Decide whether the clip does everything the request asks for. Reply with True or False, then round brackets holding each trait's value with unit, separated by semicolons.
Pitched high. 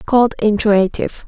True (215 Hz)